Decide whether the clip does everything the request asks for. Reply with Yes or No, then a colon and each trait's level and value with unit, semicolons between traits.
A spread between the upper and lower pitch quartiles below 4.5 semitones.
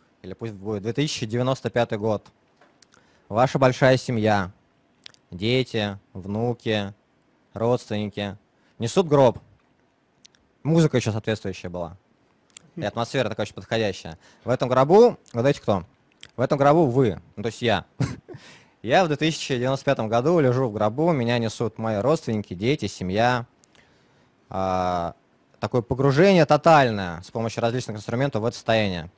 Yes: average, 4.1 semitones